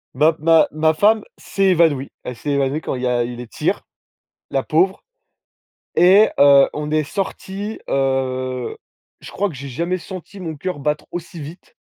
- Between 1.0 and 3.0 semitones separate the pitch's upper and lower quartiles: No, average, 5.0 semitones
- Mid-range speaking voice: Yes, medium, 155 Hz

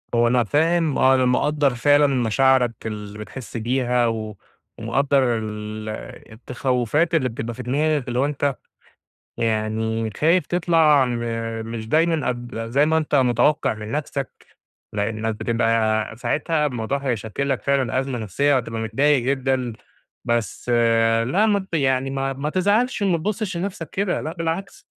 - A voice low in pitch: Yes, low, 130 Hz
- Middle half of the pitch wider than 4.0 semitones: Yes, average, 4.6 semitones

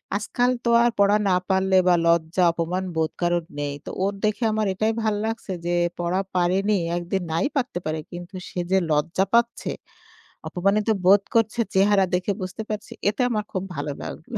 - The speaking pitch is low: No, high, 190 Hz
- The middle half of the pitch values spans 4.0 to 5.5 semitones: No, average, 3.4 semitones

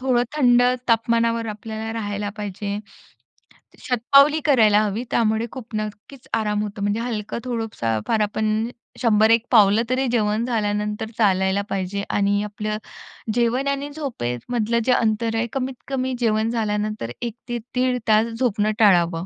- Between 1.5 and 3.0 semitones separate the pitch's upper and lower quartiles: Yes, narrow, 2.5 semitones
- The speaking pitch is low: No, high, 220 Hz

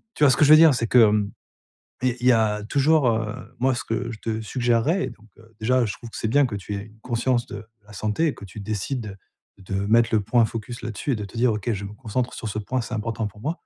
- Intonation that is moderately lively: Yes, average, 3.0 semitones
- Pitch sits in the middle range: No, low, 115 Hz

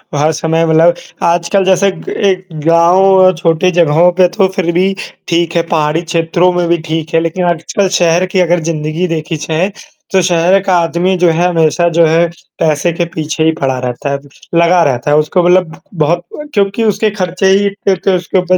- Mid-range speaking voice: Yes, medium, 170 Hz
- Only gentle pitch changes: Yes, narrow, 2.2 semitones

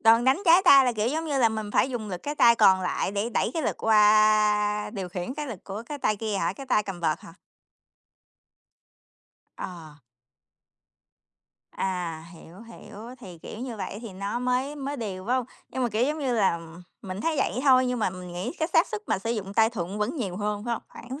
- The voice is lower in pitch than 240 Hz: Yes, high, 220 Hz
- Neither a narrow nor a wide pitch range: Yes, average, 4.7 semitones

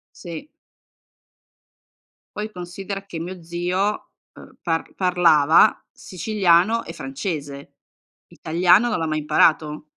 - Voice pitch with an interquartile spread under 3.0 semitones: No, average, 3.5 semitones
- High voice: No, medium, 175 Hz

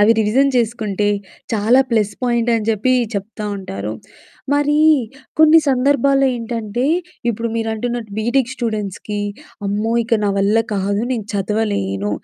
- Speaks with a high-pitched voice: Yes, high, 225 Hz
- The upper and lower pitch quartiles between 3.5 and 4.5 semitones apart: No, average, 2.9 semitones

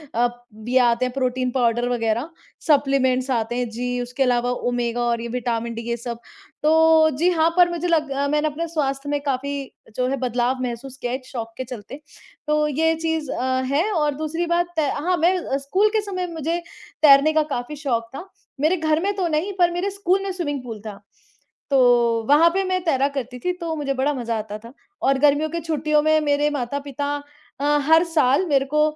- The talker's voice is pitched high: Yes, very high, 280 Hz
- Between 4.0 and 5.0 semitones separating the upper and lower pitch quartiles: Yes, average, 4.4 semitones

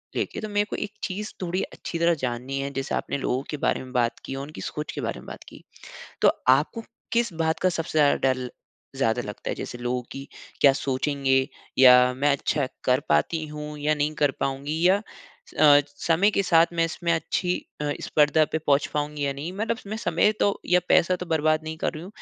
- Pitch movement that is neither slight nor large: Yes, average, 3.8 semitones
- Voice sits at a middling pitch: Yes, medium, 150 Hz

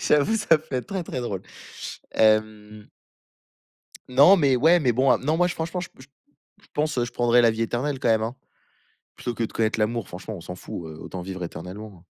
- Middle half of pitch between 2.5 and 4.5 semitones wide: No, average, 5.3 semitones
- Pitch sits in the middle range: No, low, 120 Hz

